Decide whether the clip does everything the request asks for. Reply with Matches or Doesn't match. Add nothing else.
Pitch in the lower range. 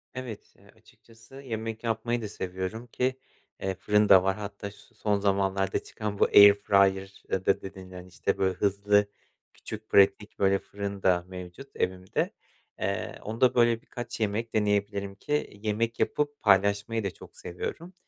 Matches